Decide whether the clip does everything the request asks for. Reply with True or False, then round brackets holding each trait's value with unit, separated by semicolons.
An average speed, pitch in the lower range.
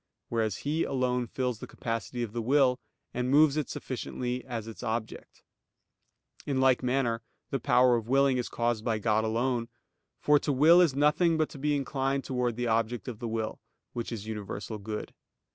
True (180 wpm; 125 Hz)